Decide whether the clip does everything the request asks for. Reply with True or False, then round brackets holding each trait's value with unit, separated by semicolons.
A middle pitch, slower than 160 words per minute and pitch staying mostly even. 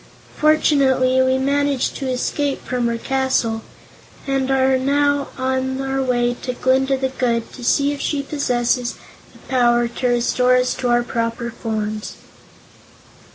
False (260 Hz; 150 wpm; 1.9 semitones)